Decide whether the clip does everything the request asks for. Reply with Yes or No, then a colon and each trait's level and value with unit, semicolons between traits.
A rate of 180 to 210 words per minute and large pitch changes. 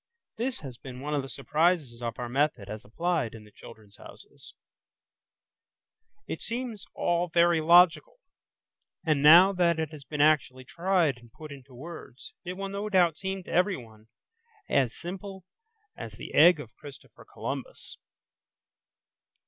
No: average, 150 wpm; wide, 5.8 semitones